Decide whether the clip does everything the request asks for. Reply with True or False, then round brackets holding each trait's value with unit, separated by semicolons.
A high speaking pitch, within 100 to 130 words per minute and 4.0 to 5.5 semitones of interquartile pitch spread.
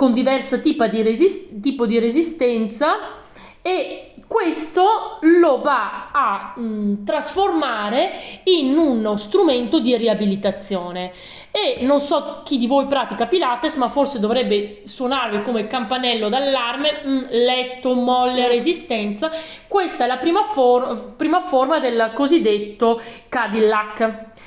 True (255 Hz; 120 wpm; 5.2 semitones)